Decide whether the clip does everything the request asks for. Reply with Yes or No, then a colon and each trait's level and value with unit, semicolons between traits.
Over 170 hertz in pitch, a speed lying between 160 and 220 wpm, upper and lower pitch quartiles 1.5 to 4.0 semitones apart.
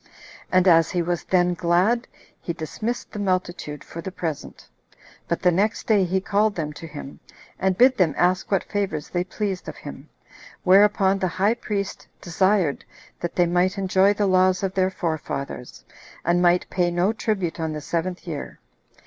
Yes: medium, 185 Hz; average, 175 wpm; narrow, 2.5 semitones